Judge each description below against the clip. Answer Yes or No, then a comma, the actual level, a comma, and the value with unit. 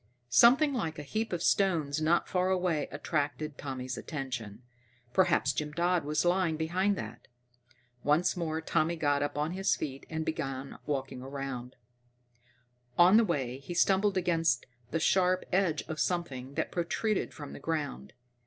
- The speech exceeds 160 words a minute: No, average, 155 wpm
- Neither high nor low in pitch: Yes, medium, 160 Hz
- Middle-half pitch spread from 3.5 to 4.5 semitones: Yes, average, 4.2 semitones